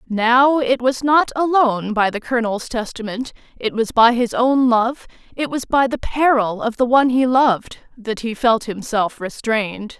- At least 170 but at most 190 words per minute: Yes, average, 180 wpm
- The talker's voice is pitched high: Yes, high, 235 Hz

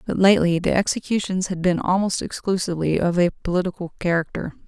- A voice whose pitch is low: No, medium, 180 Hz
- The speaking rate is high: No, average, 155 wpm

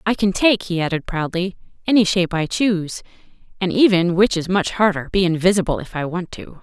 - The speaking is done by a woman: Yes, female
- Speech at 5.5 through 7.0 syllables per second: Yes, 5.8 syllables/s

